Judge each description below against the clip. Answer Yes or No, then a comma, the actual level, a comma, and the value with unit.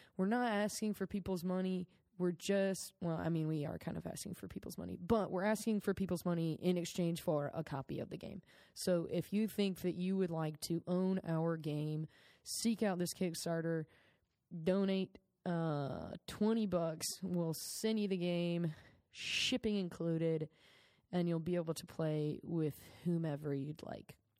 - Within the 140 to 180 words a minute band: Yes, average, 170 wpm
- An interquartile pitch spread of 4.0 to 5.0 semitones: No, average, 3.0 semitones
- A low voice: No, medium, 175 Hz